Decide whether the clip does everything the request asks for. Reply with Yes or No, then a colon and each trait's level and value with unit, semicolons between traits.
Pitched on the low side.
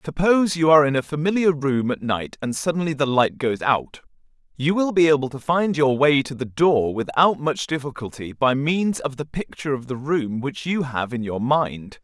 No: medium, 145 Hz